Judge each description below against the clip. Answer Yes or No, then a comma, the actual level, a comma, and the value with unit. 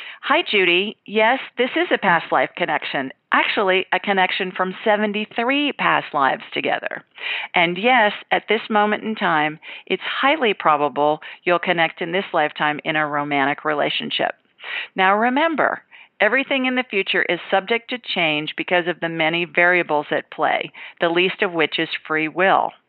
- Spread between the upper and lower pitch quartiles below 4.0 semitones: No, average, 5.0 semitones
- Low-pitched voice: No, medium, 185 Hz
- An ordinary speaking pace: Yes, average, 155 wpm